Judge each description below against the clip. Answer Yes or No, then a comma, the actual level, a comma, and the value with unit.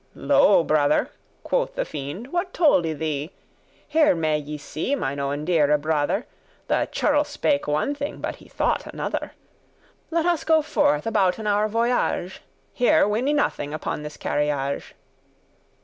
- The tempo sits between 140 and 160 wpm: Yes, average, 150 wpm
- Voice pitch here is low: No, high, 190 Hz